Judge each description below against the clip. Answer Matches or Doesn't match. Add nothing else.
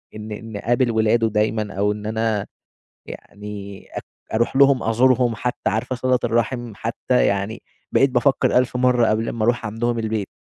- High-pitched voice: Doesn't match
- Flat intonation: Matches